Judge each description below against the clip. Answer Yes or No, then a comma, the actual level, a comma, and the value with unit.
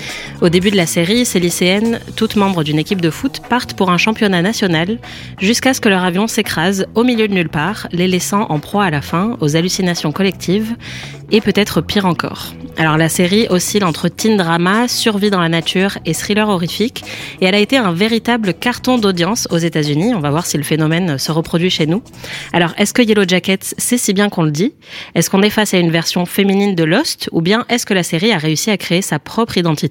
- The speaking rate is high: Yes, fast, 225 wpm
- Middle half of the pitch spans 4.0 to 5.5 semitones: Yes, average, 4.3 semitones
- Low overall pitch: No, high, 190 Hz